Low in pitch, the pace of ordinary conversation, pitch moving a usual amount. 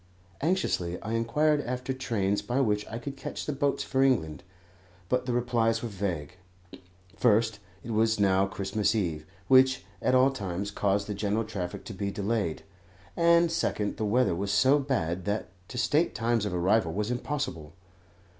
Yes: low, 110 Hz; average, 165 wpm; average, 4.5 semitones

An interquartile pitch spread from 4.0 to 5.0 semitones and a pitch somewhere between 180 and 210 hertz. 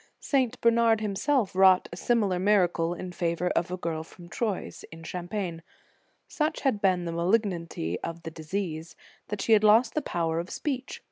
Yes: average, 4.6 semitones; medium, 185 Hz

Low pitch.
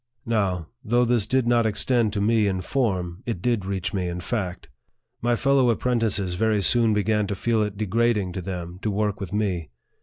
Yes: low, 105 Hz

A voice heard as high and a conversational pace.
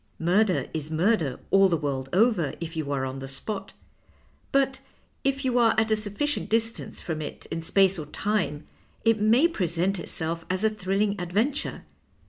Yes: high, 195 Hz; average, 170 wpm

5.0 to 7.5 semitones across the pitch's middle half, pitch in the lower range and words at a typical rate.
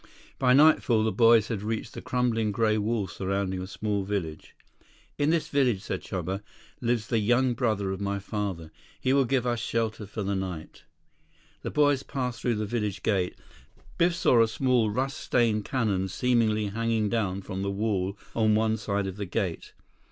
No: average, 3.3 semitones; low, 110 Hz; average, 180 wpm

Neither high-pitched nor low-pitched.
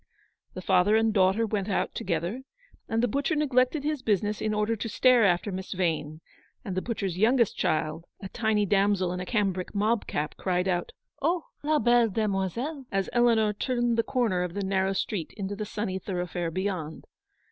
No: high, 205 Hz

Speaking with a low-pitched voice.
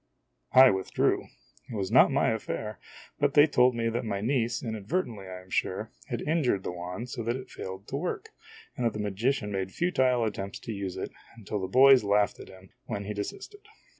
Yes: low, 110 Hz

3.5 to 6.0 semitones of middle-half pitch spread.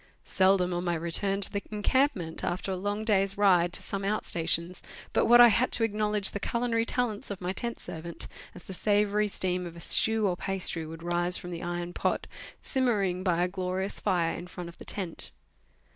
No: average, 3.1 semitones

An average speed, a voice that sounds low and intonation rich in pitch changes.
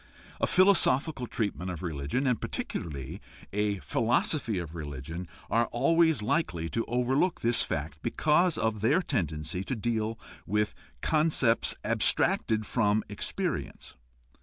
No: slow, 120 wpm; low, 110 Hz; wide, 6.9 semitones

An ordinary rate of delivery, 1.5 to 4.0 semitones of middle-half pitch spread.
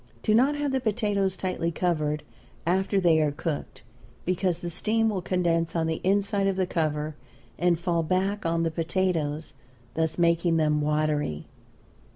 Yes: average, 160 wpm; average, 3.3 semitones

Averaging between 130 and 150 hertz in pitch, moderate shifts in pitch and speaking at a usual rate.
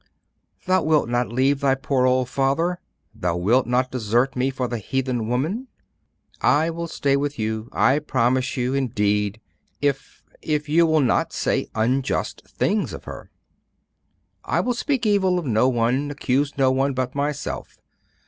Yes: low, 135 Hz; average, 3.1 semitones; average, 160 wpm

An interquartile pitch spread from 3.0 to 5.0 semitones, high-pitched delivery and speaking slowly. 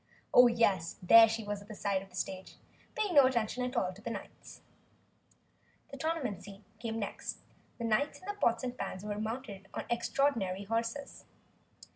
No: average, 3.9 semitones; high, 225 Hz; average, 180 wpm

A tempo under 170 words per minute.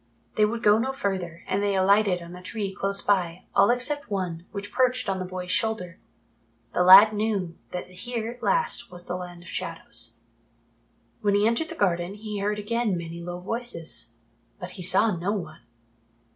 No: average, 185 wpm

